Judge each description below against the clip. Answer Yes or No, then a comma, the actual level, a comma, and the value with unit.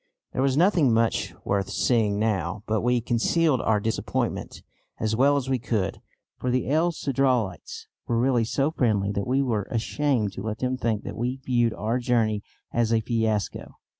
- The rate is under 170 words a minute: No, average, 175 wpm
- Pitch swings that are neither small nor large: Yes, average, 3.2 semitones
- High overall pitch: No, low, 115 Hz